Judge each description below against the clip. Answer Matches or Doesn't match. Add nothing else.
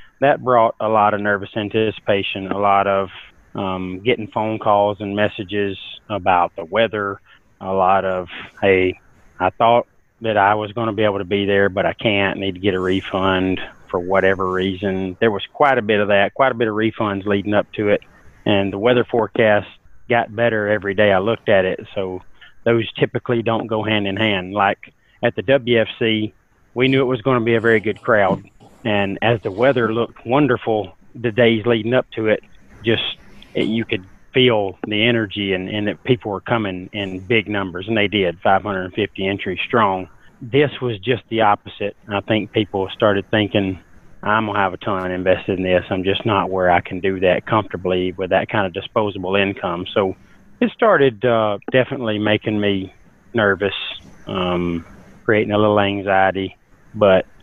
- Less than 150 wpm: Doesn't match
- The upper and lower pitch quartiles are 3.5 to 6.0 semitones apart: Doesn't match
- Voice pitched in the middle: Doesn't match